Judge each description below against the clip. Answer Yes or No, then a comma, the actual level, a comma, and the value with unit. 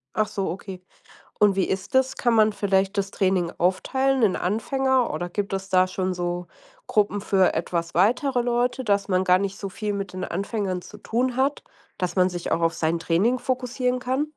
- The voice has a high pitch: Yes, high, 200 Hz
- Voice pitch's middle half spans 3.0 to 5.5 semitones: Yes, average, 4.9 semitones